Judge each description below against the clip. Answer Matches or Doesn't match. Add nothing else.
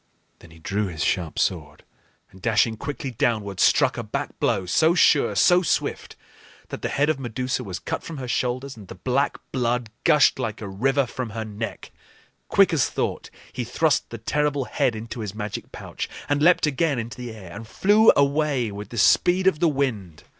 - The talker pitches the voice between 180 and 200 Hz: Doesn't match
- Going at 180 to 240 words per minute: Matches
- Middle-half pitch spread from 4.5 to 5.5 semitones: Matches